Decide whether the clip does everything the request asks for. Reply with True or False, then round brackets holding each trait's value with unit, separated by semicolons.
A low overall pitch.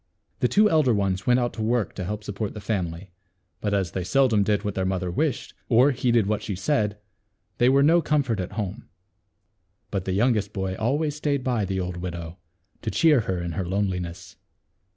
True (105 Hz)